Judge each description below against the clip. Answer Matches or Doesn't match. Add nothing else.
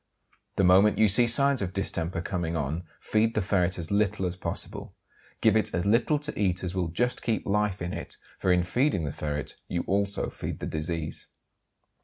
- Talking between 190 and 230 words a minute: Matches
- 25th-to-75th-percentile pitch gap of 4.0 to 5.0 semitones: Doesn't match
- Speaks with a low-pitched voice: Matches